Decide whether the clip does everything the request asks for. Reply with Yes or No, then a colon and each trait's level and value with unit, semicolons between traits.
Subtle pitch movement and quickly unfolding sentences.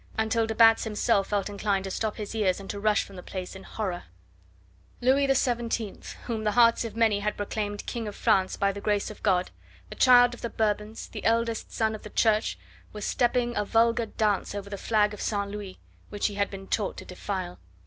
Yes: narrow, 2.2 semitones; fast, 215 wpm